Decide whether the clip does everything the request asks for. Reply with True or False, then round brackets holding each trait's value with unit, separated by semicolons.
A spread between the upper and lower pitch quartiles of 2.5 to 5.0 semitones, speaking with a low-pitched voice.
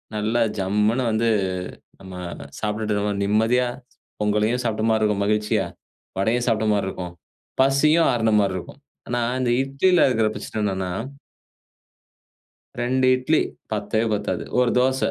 True (3.1 semitones; 110 Hz)